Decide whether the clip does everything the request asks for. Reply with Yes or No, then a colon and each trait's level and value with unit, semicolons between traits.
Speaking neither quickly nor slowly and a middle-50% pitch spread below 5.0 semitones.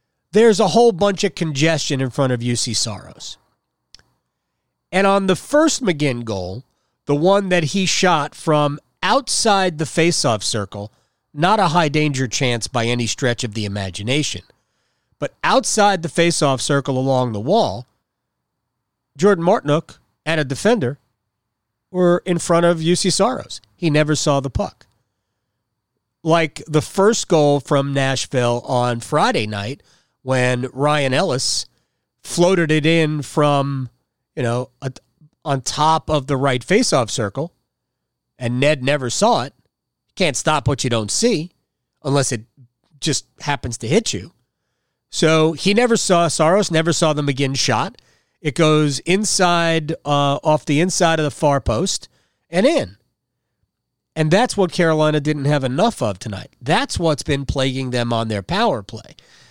No: average, 145 wpm; average, 5.3 semitones